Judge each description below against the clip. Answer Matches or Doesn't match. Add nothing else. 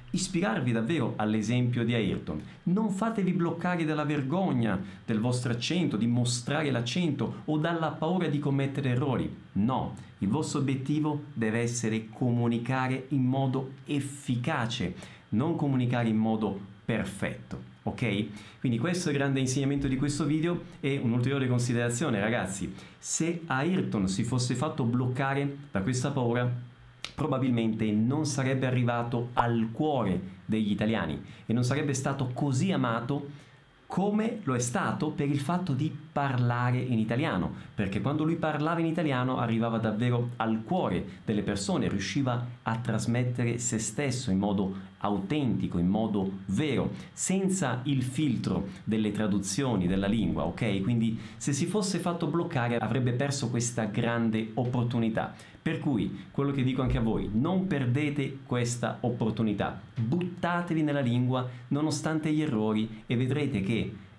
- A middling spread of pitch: Matches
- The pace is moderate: Matches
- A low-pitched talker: Matches